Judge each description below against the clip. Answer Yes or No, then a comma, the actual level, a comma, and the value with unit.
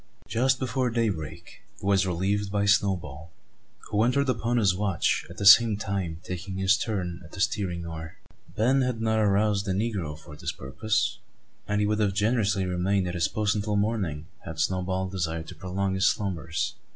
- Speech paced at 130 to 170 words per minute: No, average, 180 wpm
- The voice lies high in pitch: No, low, 100 Hz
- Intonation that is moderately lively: Yes, average, 3.4 semitones